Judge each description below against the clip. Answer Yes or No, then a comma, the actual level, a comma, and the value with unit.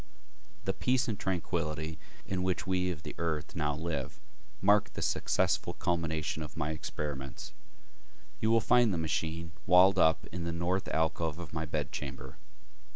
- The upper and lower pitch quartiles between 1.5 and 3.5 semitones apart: Yes, average, 2.9 semitones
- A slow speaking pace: No, average, 155 wpm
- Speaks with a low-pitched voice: Yes, very low, 80 Hz